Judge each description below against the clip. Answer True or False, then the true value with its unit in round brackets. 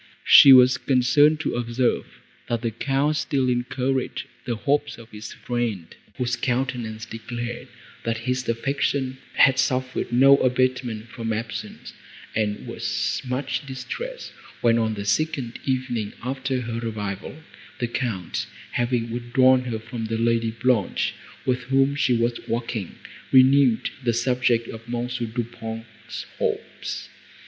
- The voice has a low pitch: True (120 Hz)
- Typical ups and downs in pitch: False (2.2 semitones)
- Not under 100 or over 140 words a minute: True (135 wpm)